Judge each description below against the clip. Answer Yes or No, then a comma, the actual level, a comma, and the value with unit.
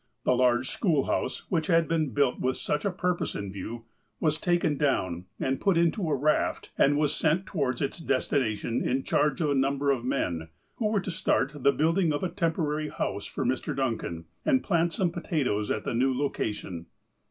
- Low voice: No, medium, 145 Hz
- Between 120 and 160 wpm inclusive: No, average, 195 wpm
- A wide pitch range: No, average, 4.8 semitones